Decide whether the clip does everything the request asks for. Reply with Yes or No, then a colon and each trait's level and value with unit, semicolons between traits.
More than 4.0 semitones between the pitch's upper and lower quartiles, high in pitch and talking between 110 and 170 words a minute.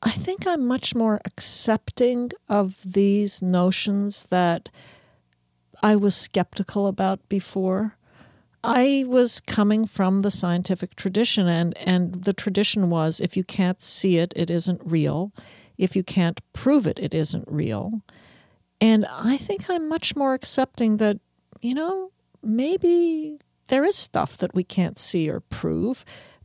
Yes: average, 4.5 semitones; high, 200 Hz; average, 145 wpm